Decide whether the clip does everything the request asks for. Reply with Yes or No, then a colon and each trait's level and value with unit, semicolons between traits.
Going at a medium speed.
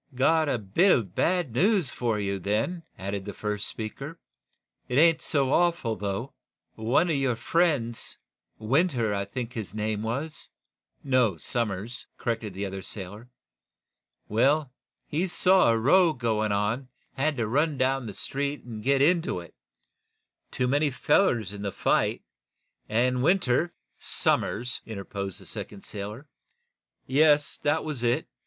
Yes: average, 155 wpm